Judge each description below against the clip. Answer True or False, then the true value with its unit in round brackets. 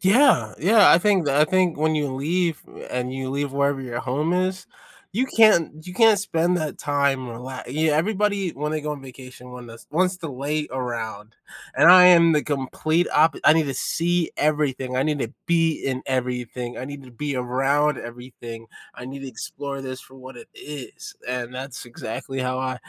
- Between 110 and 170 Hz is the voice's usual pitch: True (140 Hz)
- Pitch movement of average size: True (4.2 semitones)